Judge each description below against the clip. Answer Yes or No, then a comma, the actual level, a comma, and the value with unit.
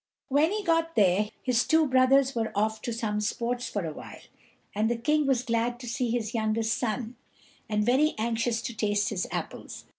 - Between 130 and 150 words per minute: No, average, 190 wpm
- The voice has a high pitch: Yes, high, 235 Hz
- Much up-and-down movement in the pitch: No, average, 3.1 semitones